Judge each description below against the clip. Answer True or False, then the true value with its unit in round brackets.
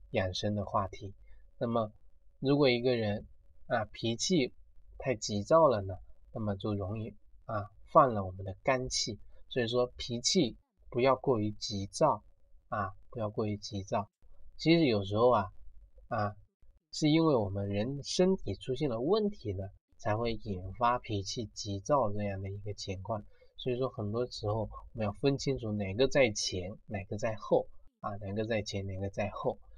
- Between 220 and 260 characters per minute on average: True (235 characters per minute)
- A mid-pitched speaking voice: False (105 Hz)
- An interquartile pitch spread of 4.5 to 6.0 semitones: False (3.8 semitones)